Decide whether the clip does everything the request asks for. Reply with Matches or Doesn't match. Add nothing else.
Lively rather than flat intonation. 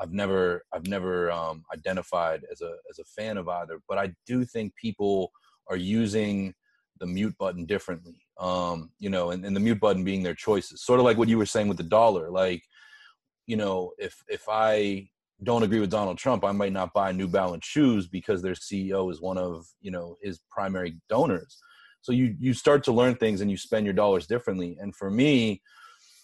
Doesn't match